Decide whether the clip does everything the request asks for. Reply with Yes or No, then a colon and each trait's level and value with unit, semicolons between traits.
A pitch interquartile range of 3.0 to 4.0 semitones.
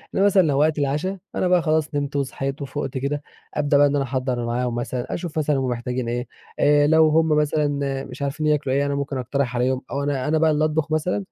No: narrow, 2.5 semitones